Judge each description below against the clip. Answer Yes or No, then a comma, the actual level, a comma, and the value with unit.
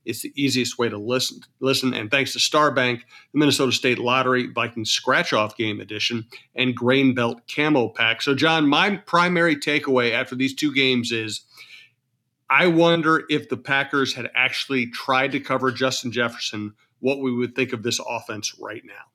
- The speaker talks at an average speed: Yes, average, 175 wpm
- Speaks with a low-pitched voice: Yes, low, 130 Hz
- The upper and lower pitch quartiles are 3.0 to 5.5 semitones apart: No, narrow, 2.6 semitones